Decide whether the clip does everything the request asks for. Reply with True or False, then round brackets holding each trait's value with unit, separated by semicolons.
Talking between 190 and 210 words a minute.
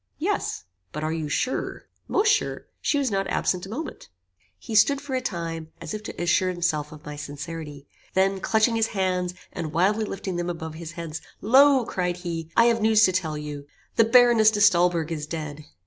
True (195 wpm)